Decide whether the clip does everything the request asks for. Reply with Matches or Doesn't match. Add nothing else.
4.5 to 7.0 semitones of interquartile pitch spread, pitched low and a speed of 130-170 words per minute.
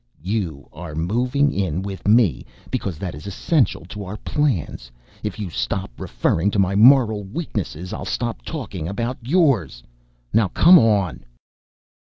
Matches